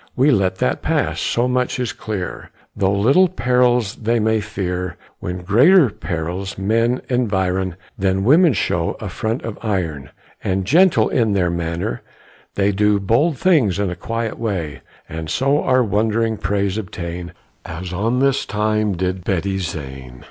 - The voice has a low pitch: Yes, low, 100 Hz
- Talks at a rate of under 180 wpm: Yes, average, 155 wpm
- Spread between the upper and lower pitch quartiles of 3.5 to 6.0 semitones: Yes, average, 4.6 semitones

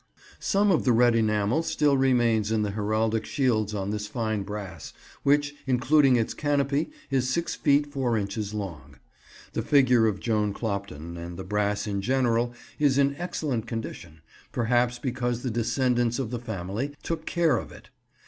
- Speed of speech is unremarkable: Yes, average, 165 wpm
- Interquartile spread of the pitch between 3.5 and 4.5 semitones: Yes, average, 4.2 semitones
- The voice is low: Yes, low, 120 Hz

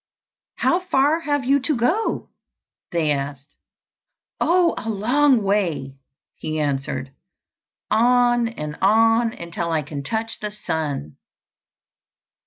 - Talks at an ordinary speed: No, slow, 110 wpm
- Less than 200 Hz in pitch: No, high, 215 Hz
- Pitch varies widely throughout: Yes, wide, 8.4 semitones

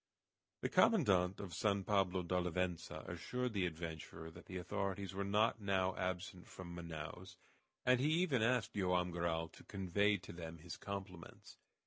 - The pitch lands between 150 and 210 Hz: No, very low, 95 Hz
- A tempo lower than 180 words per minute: Yes, average, 150 wpm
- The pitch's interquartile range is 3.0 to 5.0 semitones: No, narrow, 2.6 semitones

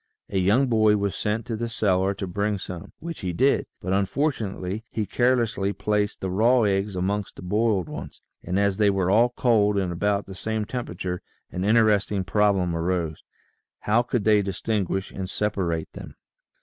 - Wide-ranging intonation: No, narrow, 2.6 semitones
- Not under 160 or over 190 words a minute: Yes, average, 175 wpm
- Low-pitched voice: Yes, low, 100 Hz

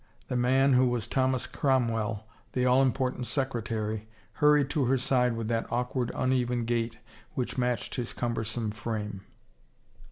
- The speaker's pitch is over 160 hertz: No, low, 125 Hz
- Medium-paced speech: Yes, average, 150 wpm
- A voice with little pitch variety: Yes, narrow, 2.3 semitones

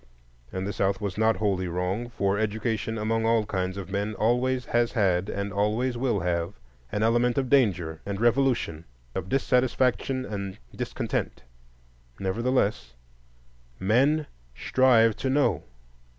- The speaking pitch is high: No, low, 110 Hz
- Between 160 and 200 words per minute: No, slow, 135 wpm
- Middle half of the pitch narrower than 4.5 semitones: Yes, average, 3.9 semitones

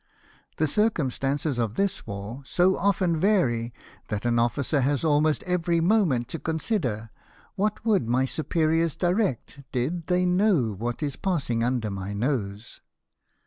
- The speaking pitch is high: No, medium, 145 Hz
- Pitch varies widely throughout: Yes, wide, 7.0 semitones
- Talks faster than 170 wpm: No, average, 140 wpm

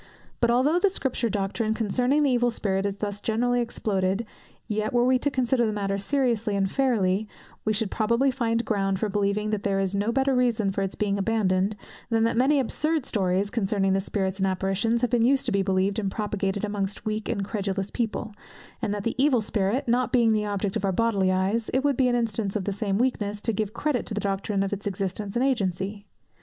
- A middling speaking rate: No, fast, 215 wpm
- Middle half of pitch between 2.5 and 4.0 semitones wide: Yes, average, 3.4 semitones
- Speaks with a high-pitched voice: Yes, high, 210 Hz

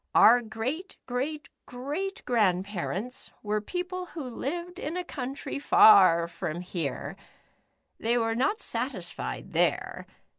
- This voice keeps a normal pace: No, slow, 115 wpm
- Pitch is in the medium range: No, high, 245 Hz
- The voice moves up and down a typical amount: No, wide, 6.8 semitones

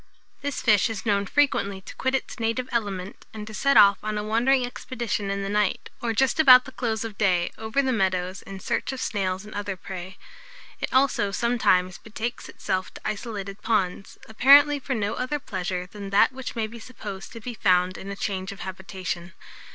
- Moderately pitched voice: No, high, 210 Hz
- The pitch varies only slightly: No, average, 3.9 semitones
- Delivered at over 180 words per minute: Yes, average, 200 wpm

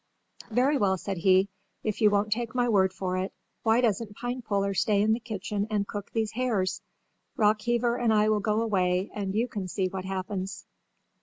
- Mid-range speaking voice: No, high, 210 Hz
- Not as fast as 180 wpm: No, average, 185 wpm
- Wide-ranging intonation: No, average, 2.8 semitones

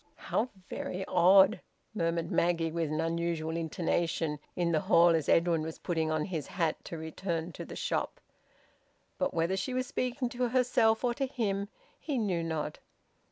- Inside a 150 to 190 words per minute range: Yes, average, 165 wpm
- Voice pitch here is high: No, medium, 170 Hz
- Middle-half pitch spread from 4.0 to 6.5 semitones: Yes, average, 4.5 semitones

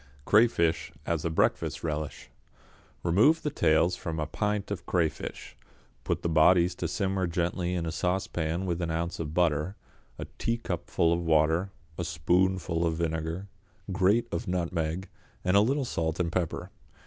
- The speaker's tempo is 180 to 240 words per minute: No, average, 155 wpm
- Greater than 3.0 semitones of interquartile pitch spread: No, narrow, 2.5 semitones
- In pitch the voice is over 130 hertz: No, very low, 85 Hz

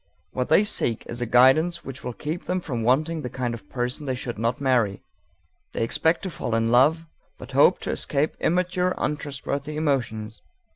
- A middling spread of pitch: Yes, average, 4.8 semitones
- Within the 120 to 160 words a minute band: No, average, 185 wpm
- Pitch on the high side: No, low, 135 Hz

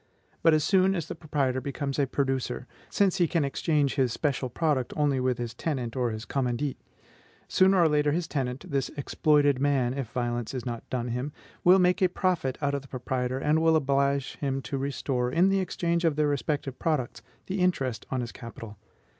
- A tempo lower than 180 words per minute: No, average, 195 wpm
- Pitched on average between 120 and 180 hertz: Yes, medium, 140 Hz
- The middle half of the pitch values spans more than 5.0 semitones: No, average, 3.7 semitones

